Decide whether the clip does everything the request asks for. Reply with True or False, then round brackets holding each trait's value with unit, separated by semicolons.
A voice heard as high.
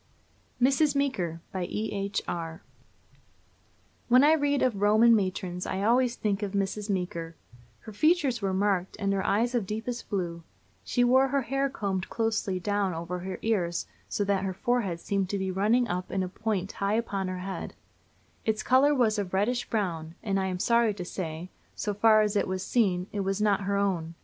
True (200 Hz)